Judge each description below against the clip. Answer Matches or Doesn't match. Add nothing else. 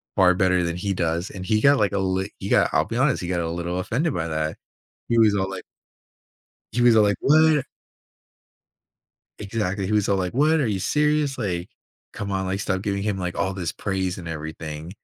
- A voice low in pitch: Matches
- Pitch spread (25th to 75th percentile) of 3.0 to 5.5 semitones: Matches